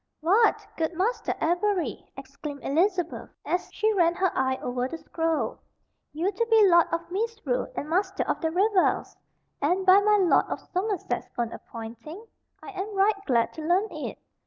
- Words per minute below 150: No, average, 165 wpm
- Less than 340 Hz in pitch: No, very high, 360 Hz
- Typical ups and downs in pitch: Yes, average, 4.5 semitones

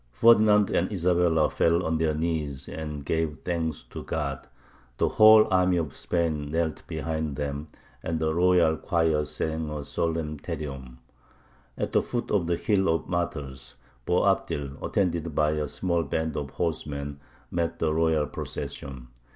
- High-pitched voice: No, very low, 80 Hz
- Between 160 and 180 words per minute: No, average, 150 wpm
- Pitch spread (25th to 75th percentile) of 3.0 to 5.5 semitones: No, narrow, 2.5 semitones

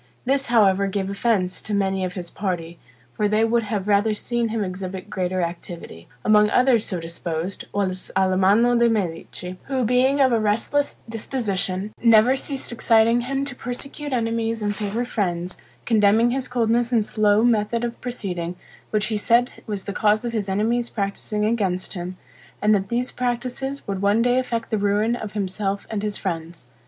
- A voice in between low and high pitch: No, high, 215 Hz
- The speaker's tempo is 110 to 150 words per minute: No, average, 175 wpm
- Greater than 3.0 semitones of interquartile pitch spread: Yes, average, 3.6 semitones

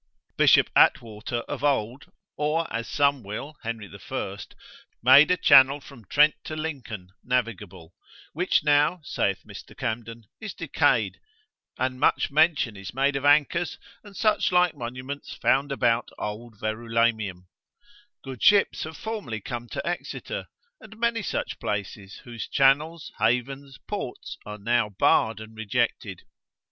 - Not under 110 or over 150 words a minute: Yes, slow, 135 wpm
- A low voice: Yes, low, 125 Hz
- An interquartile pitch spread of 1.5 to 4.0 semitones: No, average, 5.1 semitones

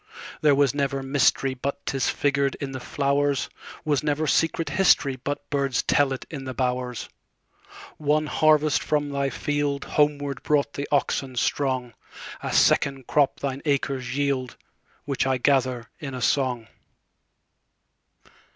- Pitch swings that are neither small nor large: No, narrow, 1.7 semitones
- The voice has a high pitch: No, medium, 140 Hz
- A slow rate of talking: Yes, slow, 115 wpm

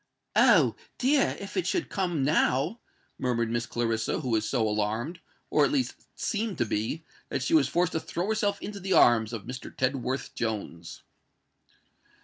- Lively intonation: Yes, wide, 8.6 semitones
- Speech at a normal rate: Yes, average, 155 wpm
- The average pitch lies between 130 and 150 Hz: Yes, low, 135 Hz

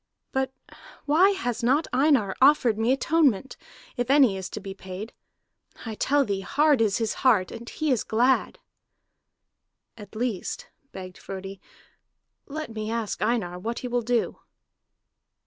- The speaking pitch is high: Yes, high, 235 Hz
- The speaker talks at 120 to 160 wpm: Yes, average, 145 wpm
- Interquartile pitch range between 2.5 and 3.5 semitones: No, average, 4.6 semitones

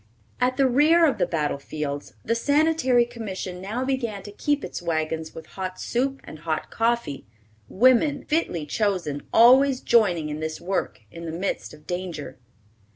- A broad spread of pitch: Yes, wide, 8.0 semitones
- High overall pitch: Yes, high, 200 Hz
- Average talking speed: Yes, average, 160 wpm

